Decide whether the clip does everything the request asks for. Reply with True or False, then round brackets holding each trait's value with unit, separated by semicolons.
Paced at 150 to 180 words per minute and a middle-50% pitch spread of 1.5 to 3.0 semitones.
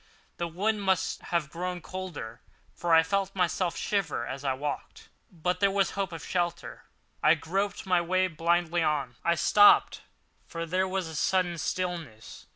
True (165 wpm; 2.5 semitones)